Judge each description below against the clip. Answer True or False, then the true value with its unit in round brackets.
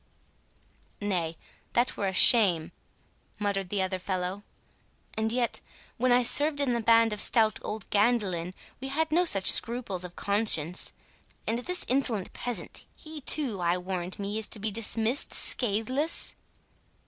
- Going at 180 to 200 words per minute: False (145 wpm)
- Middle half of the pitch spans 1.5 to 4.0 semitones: False (4.5 semitones)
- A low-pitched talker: False (215 Hz)